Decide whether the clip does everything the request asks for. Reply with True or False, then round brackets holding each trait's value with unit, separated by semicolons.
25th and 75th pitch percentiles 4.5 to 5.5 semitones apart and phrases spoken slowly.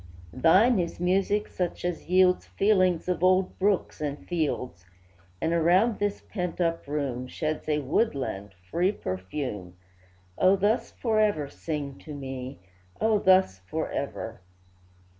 True (5.2 semitones; 125 wpm)